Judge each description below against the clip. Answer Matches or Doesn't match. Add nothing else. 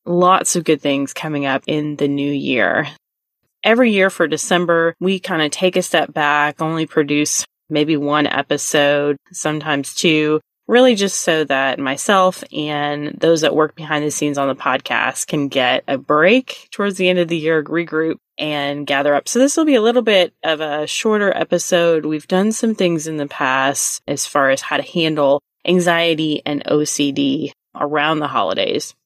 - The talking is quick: Doesn't match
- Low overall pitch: Doesn't match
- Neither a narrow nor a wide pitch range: Matches